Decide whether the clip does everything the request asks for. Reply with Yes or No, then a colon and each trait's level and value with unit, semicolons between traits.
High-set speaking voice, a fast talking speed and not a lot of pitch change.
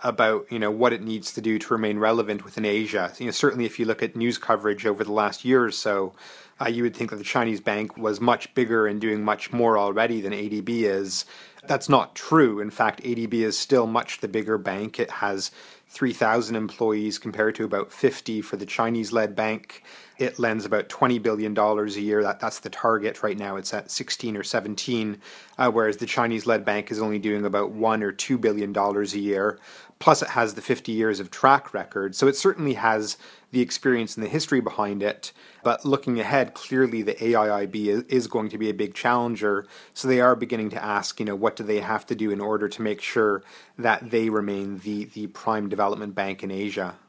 No: low, 110 Hz; fast, 215 wpm; narrow, 1.9 semitones